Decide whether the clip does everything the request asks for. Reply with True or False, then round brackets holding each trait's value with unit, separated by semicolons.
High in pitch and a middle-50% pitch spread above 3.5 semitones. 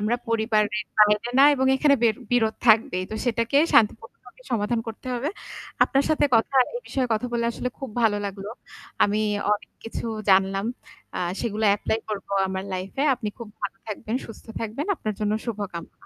False (220 Hz; 2.4 semitones)